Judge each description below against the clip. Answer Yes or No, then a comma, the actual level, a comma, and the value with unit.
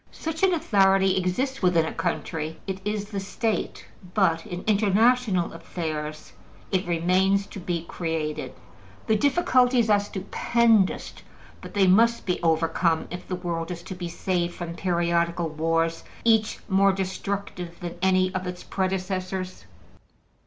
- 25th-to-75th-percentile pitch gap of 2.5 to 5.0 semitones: Yes, average, 3.0 semitones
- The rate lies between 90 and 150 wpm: Yes, average, 140 wpm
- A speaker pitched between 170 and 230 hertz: Yes, medium, 185 Hz